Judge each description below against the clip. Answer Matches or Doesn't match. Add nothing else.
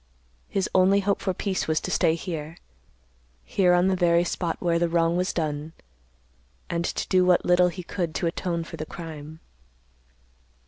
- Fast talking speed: Doesn't match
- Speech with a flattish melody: Matches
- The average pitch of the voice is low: Doesn't match